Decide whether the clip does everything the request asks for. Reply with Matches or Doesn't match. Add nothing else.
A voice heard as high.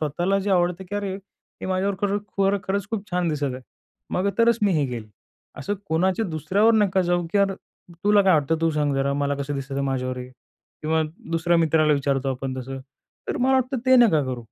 Doesn't match